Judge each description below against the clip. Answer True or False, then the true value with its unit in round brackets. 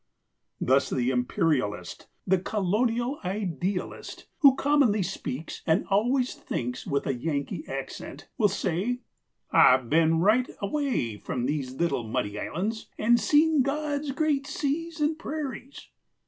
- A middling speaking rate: False (125 wpm)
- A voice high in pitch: True (205 Hz)